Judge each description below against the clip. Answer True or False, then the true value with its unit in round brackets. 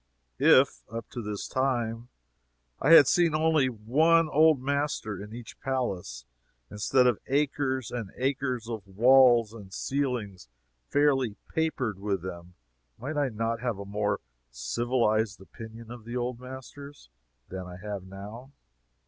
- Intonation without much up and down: False (4.4 semitones)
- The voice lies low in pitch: True (120 Hz)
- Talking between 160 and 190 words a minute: False (140 wpm)